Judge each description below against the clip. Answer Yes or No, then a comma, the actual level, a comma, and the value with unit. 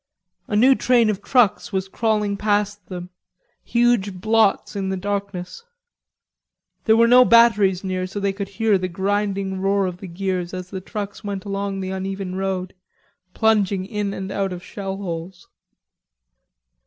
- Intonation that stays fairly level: Yes, narrow, 1.8 semitones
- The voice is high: Yes, high, 195 Hz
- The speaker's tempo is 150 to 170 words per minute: Yes, average, 155 wpm